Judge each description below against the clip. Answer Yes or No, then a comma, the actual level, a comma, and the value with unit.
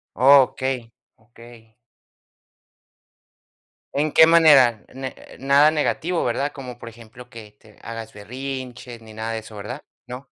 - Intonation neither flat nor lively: Yes, average, 3.2 semitones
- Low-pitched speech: Yes, low, 125 Hz